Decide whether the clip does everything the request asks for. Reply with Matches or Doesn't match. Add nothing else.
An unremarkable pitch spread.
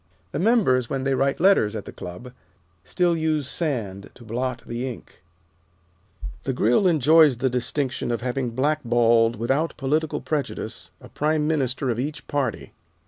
Matches